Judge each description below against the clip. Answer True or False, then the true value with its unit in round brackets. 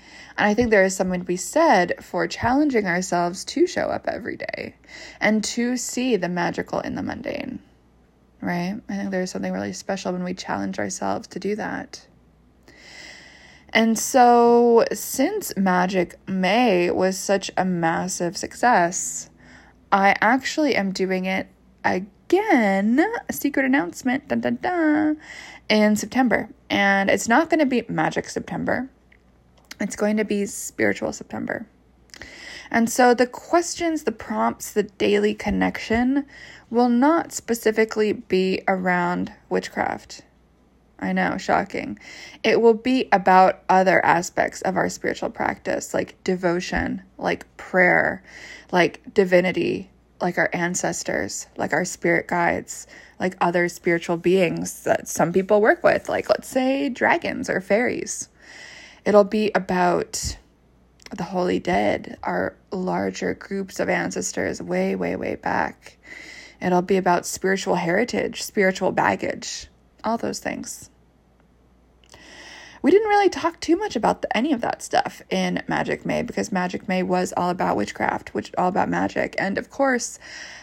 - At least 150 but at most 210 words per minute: False (140 wpm)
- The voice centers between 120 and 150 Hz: False (195 Hz)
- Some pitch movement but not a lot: False (5.8 semitones)